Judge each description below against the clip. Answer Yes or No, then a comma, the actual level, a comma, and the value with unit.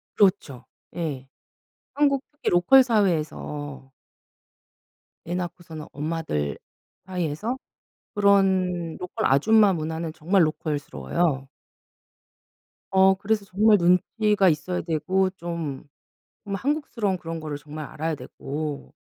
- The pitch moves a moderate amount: Yes, average, 4.4 semitones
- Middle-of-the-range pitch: Yes, medium, 175 Hz